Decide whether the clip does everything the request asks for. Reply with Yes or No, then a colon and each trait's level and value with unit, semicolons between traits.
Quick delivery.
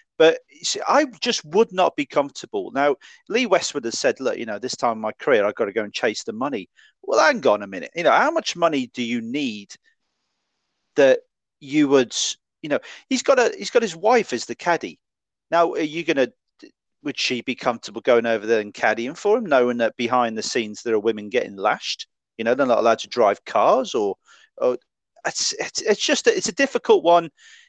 Yes: fast, 220 wpm